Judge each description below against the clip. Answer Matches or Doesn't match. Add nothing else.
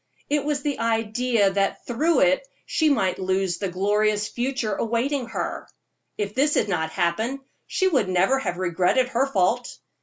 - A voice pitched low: Doesn't match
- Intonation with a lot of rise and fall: Matches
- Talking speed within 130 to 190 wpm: Matches